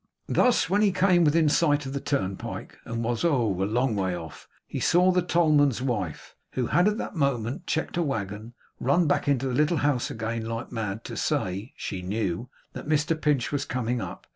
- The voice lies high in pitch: No, low, 135 Hz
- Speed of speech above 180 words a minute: Yes, average, 195 wpm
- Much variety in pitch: Yes, wide, 5.7 semitones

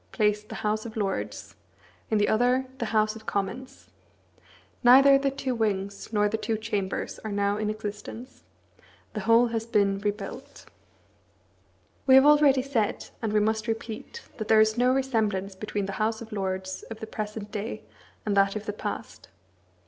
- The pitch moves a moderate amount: No, narrow, 2.1 semitones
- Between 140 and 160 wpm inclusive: No, average, 170 wpm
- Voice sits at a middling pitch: No, high, 215 Hz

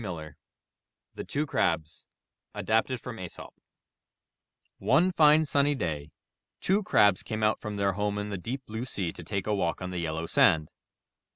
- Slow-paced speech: No, average, 170 wpm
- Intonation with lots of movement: Yes, wide, 6.8 semitones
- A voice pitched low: Yes, low, 105 Hz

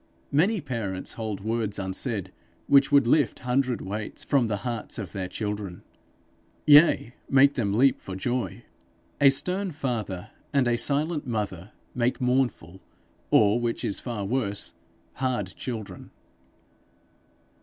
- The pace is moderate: No, slow, 130 wpm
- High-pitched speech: No, low, 120 Hz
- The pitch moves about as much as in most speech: Yes, average, 4.9 semitones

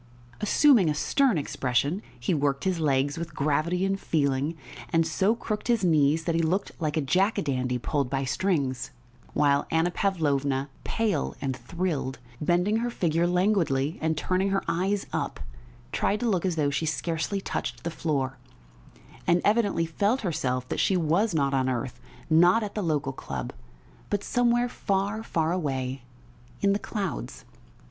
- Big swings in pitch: Yes, wide, 5.7 semitones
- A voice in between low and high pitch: Yes, medium, 165 Hz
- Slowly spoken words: No, average, 165 wpm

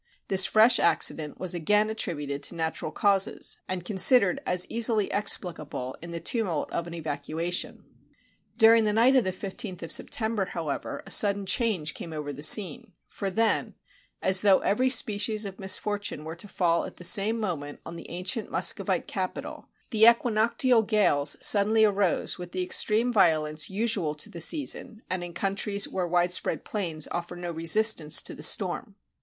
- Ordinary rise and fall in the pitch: Yes, average, 4.3 semitones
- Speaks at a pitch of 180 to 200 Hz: Yes, high, 190 Hz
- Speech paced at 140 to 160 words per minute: No, average, 170 wpm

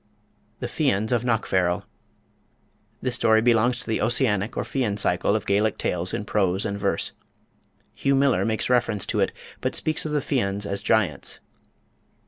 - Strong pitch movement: No, average, 3.8 semitones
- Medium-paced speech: Yes, average, 160 wpm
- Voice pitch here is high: No, low, 110 Hz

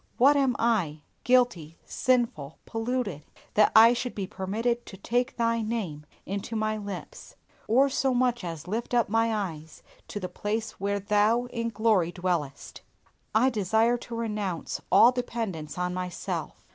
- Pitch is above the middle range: Yes, high, 215 Hz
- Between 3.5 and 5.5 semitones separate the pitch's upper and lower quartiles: Yes, average, 4.4 semitones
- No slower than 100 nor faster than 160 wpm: Yes, average, 150 wpm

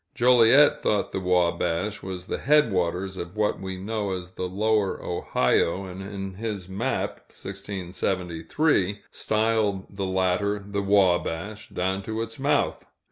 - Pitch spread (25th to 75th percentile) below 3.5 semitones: Yes, narrow, 2.6 semitones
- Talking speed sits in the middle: No, slow, 130 wpm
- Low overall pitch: Yes, very low, 95 Hz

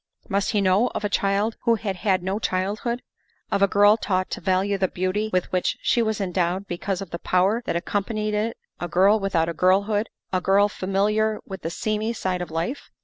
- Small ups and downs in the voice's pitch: Yes, narrow, 2.3 semitones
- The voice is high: Yes, high, 195 Hz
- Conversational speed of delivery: No, fast, 210 wpm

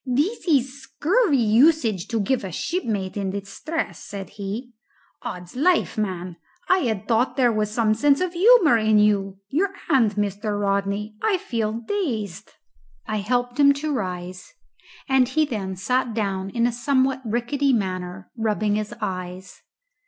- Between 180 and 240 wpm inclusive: No, average, 150 wpm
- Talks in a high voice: Yes, high, 225 Hz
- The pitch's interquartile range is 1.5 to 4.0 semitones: No, average, 5.2 semitones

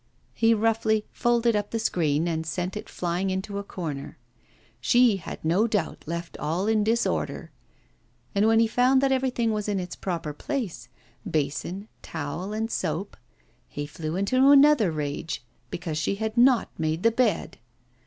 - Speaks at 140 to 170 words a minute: Yes, average, 160 wpm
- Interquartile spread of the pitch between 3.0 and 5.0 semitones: No, wide, 5.5 semitones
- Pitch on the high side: Yes, high, 200 Hz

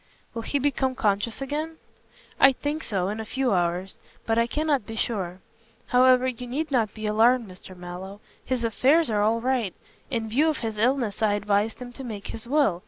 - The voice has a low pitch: No, high, 230 Hz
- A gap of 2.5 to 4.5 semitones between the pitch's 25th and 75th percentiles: Yes, average, 4.1 semitones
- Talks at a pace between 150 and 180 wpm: No, average, 195 wpm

